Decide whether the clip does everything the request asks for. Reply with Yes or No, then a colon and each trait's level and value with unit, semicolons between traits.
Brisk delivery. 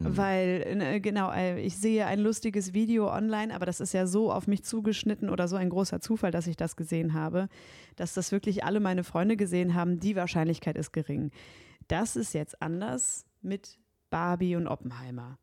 No: average, 180 wpm